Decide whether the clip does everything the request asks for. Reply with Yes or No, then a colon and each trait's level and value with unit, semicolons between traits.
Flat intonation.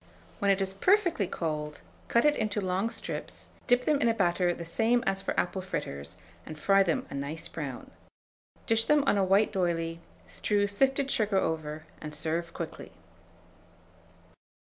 No: wide, 5.4 semitones